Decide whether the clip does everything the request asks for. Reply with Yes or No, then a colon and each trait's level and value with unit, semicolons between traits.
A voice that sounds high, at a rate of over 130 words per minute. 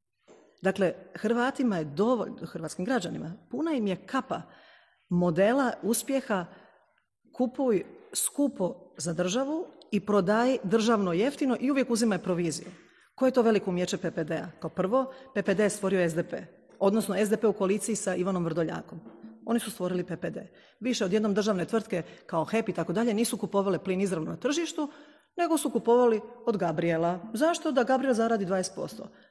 Yes: high, 210 Hz; average, 150 wpm